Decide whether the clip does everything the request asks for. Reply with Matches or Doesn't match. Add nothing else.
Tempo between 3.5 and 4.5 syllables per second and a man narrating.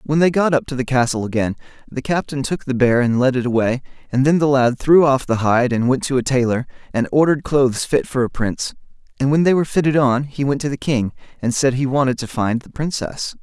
Doesn't match